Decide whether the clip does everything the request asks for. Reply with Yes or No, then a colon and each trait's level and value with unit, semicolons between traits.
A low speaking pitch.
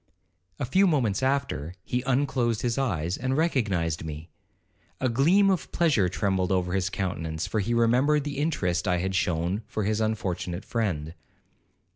Yes: low, 110 Hz